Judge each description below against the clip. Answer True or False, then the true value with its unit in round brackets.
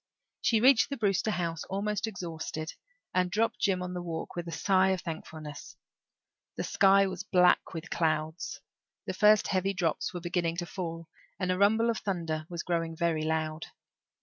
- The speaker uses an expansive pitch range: False (3.2 semitones)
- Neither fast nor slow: True (175 wpm)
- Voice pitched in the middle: True (180 Hz)